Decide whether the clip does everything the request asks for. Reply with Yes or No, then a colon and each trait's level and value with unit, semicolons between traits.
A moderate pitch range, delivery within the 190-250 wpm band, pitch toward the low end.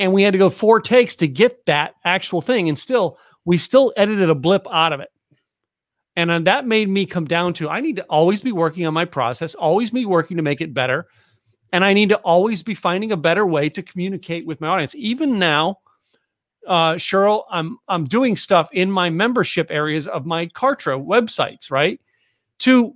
No: average, 4.5 semitones; fast, 205 wpm; medium, 180 Hz